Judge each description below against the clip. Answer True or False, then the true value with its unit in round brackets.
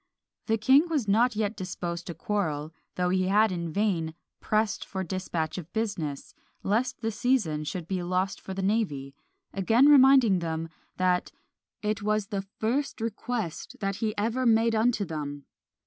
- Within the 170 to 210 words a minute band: False (160 wpm)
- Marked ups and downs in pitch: False (4.3 semitones)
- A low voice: False (200 Hz)